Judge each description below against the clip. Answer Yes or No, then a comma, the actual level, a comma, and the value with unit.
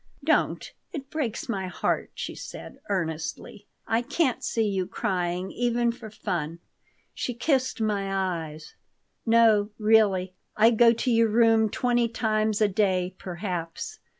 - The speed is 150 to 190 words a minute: No, slow, 135 wpm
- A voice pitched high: Yes, high, 215 Hz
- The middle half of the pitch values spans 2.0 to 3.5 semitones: No, average, 3.9 semitones